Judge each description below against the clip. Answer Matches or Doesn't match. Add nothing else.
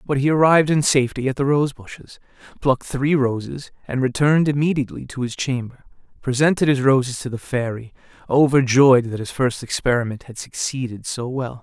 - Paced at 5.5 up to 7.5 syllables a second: Matches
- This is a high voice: Doesn't match